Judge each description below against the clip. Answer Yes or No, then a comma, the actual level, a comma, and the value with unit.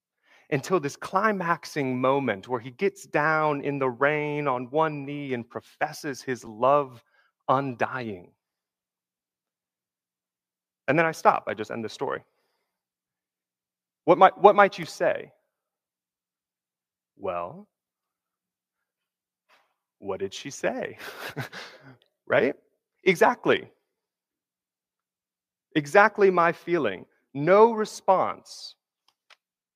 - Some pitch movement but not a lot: No, wide, 6.4 semitones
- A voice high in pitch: No, medium, 150 Hz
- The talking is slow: Yes, slow, 95 wpm